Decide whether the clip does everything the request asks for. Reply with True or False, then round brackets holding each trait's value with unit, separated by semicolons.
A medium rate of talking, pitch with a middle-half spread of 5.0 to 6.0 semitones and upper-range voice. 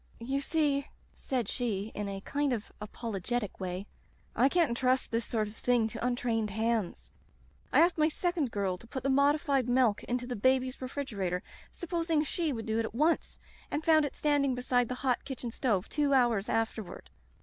False (190 wpm; 4.2 semitones; 245 Hz)